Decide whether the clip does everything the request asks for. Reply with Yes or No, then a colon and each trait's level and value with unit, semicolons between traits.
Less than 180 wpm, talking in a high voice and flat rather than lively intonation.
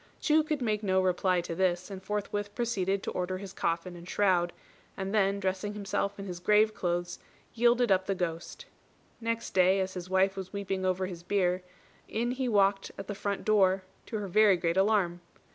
No: average, 195 wpm; high, 195 Hz; narrow, 2.2 semitones